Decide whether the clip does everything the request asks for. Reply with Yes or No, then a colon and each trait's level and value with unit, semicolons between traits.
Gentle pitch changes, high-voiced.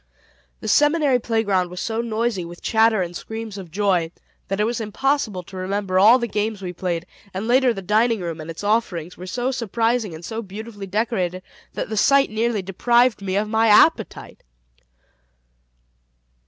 No: average, 3.8 semitones; high, 210 Hz